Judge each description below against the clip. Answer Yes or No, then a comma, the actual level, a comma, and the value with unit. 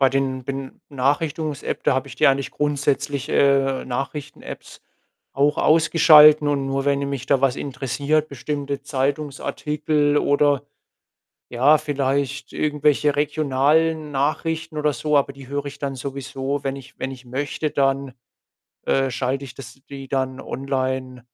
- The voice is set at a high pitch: No, medium, 140 Hz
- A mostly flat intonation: Yes, narrow, 1.6 semitones